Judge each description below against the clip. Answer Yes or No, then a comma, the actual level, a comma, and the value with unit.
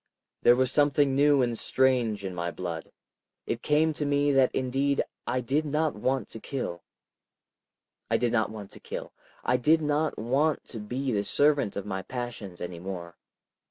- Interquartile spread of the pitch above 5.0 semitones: Yes, wide, 5.4 semitones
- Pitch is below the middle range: Yes, low, 125 Hz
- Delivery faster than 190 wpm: No, average, 175 wpm